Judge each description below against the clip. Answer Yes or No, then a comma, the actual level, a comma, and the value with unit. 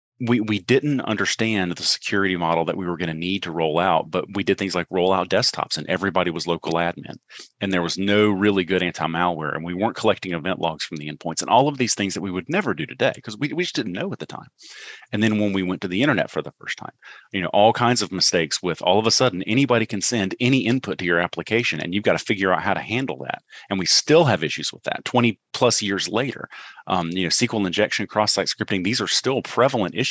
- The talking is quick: Yes, fast, 255 wpm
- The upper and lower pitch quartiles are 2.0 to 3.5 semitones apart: No, average, 4.3 semitones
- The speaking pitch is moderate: No, very low, 95 Hz